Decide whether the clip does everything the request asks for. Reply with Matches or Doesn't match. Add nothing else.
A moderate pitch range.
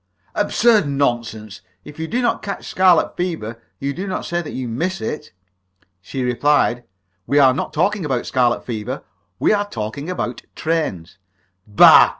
Doesn't match